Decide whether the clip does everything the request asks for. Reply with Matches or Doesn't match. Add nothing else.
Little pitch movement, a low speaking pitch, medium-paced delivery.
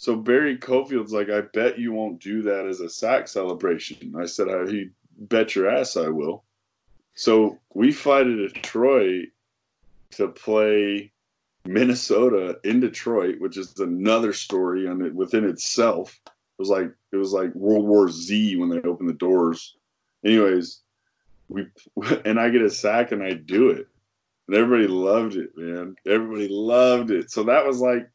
Doesn't match